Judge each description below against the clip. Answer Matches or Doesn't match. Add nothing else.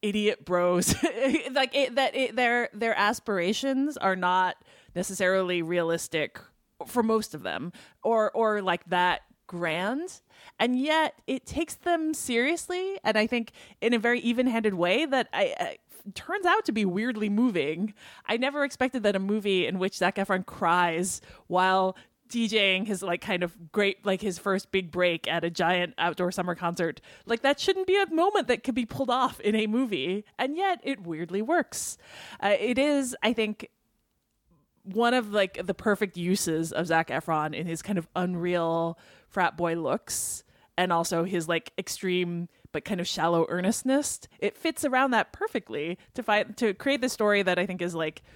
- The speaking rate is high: Doesn't match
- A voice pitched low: Doesn't match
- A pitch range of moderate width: Doesn't match